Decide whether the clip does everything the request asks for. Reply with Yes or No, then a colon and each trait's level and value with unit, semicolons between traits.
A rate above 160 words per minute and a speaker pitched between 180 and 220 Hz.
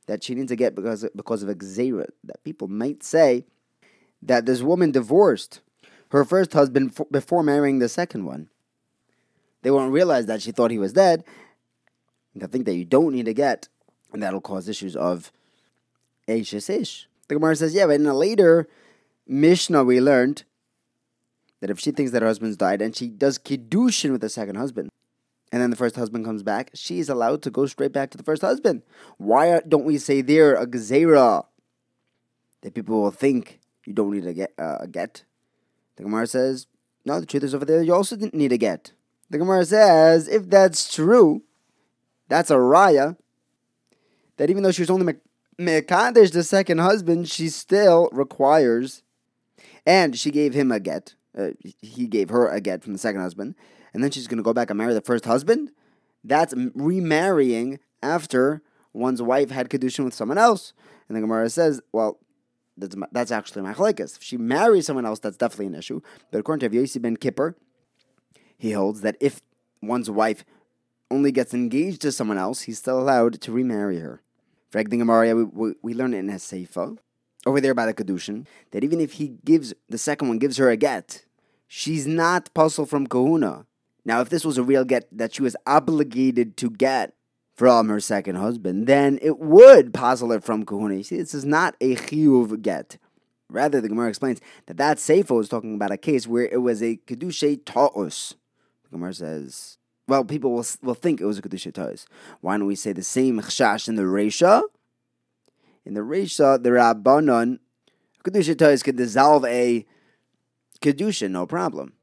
No: average, 185 wpm; low, 130 Hz